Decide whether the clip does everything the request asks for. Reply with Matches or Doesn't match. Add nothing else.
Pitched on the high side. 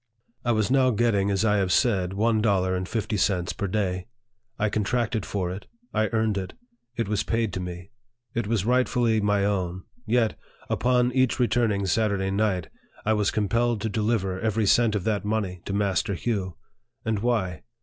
Doesn't match